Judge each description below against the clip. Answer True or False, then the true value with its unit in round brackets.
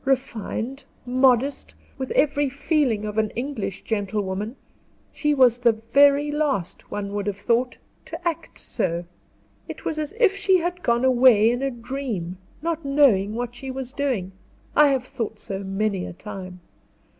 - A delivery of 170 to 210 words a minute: False (155 wpm)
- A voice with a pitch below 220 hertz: False (245 Hz)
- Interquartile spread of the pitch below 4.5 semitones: False (5.1 semitones)